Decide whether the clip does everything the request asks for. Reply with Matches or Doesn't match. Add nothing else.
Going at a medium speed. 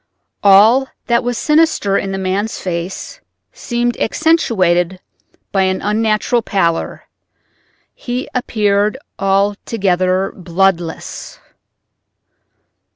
Doesn't match